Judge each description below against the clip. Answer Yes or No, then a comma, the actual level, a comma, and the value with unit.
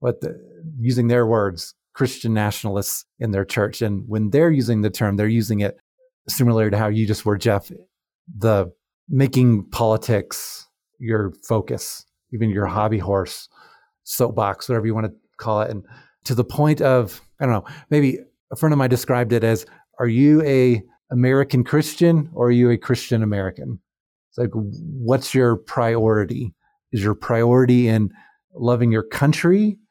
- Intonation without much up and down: No, average, 3.6 semitones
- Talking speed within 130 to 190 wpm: Yes, average, 165 wpm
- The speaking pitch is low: Yes, low, 120 Hz